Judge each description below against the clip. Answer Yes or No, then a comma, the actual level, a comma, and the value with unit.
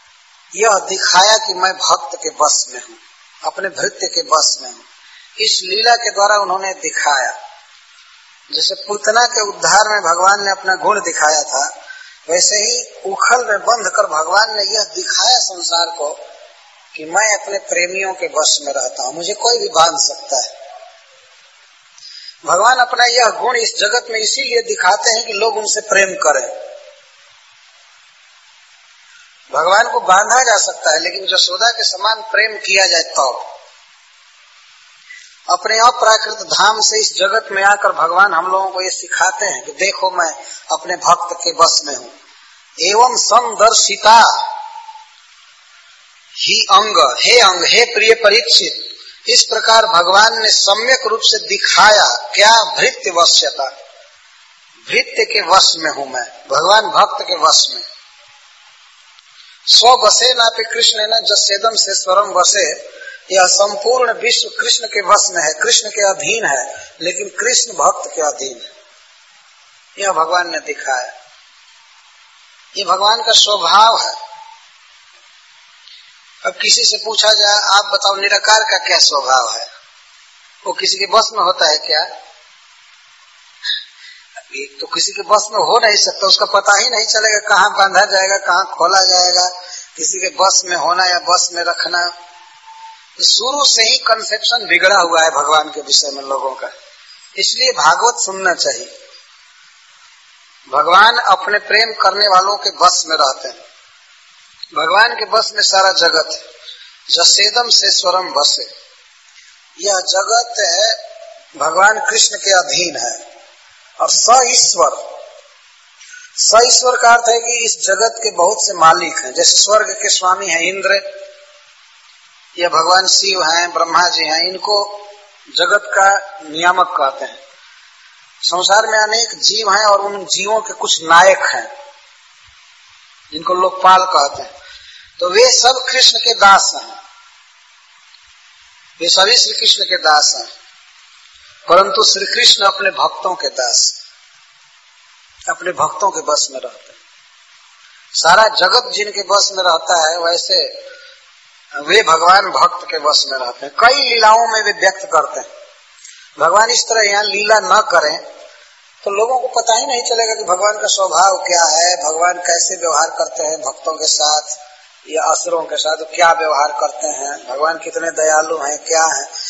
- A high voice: Yes, high, 205 Hz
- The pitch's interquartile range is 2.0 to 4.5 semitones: No, wide, 5.5 semitones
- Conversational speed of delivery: Yes, average, 150 wpm